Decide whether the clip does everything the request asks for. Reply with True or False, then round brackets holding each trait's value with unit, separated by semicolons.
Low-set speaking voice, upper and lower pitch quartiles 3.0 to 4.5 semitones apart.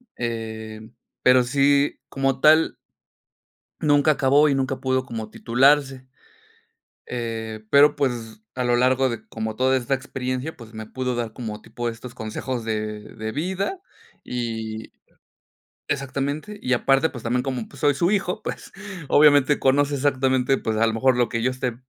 True (130 Hz; 3.4 semitones)